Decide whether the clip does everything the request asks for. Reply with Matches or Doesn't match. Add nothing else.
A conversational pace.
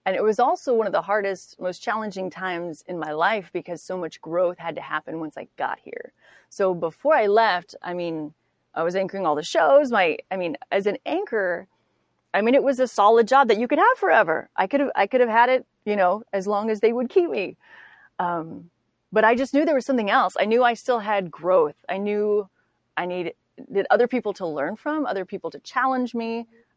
Doesn't match